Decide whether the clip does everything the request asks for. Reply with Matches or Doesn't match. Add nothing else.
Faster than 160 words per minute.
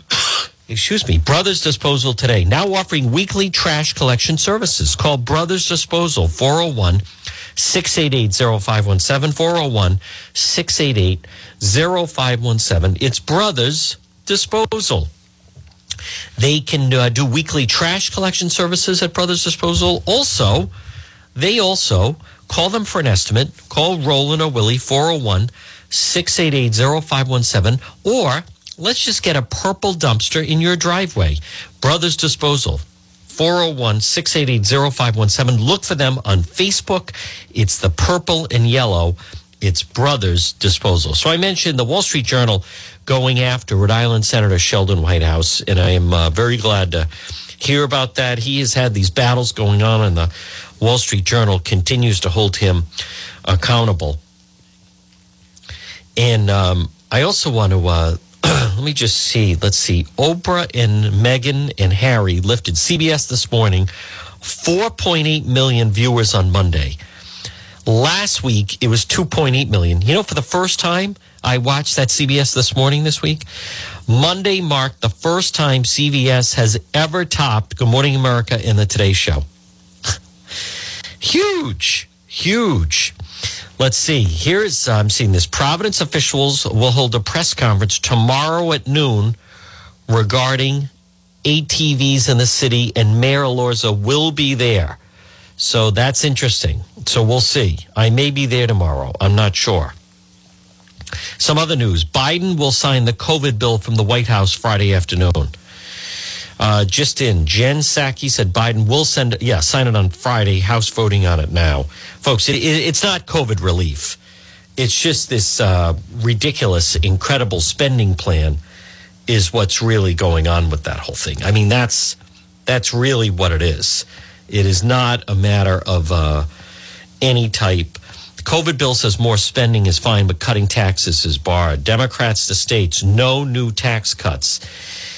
Doesn't match